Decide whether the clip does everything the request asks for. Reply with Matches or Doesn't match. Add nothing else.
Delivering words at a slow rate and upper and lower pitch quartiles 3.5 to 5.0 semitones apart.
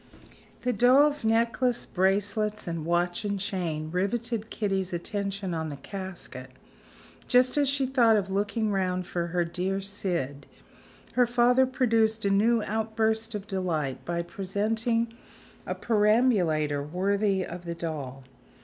Matches